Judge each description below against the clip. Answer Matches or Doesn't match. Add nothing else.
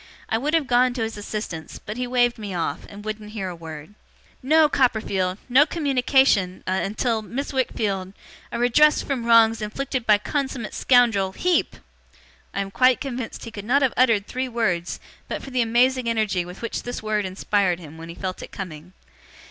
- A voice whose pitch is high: Matches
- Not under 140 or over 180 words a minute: Doesn't match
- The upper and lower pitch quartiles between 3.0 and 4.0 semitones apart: Doesn't match